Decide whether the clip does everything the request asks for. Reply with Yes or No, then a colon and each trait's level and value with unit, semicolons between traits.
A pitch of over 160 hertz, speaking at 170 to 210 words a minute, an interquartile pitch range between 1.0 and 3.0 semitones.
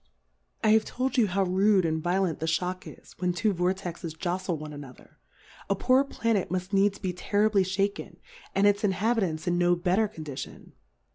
Yes: medium, 185 Hz; average, 180 wpm; average, 2.7 semitones